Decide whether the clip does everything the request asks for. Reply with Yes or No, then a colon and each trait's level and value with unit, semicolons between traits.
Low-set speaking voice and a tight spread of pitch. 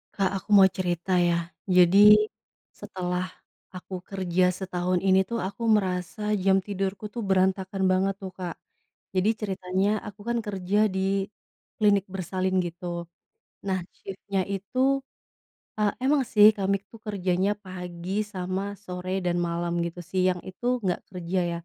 No: high, 190 Hz; narrow, 1.5 semitones